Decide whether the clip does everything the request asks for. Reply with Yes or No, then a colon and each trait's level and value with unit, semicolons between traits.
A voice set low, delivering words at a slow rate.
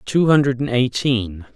Yes: low, 125 Hz; slow, 115 wpm